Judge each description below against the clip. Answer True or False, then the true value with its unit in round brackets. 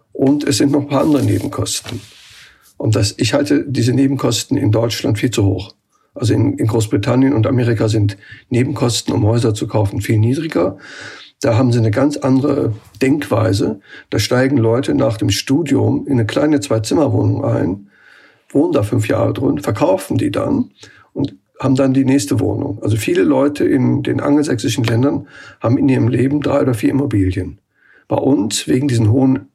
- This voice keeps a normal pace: True (175 wpm)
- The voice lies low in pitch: True (125 Hz)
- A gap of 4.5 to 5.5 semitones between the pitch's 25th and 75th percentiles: False (3.9 semitones)